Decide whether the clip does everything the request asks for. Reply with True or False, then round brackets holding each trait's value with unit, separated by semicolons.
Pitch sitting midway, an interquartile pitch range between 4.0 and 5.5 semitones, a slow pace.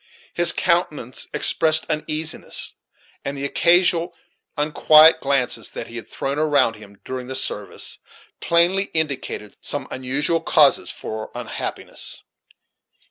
True (150 Hz; 4.4 semitones; 115 wpm)